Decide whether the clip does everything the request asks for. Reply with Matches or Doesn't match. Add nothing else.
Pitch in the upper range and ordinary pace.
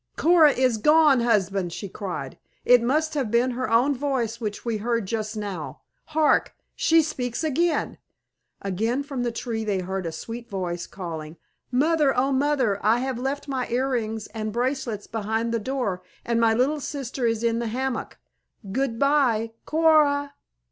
Matches